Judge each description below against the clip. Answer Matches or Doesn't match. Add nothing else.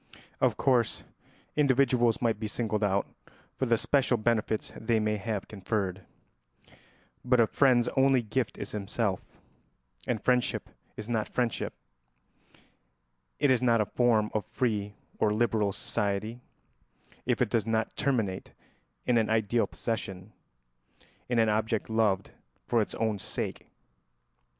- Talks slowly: Matches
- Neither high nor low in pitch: Doesn't match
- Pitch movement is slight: Matches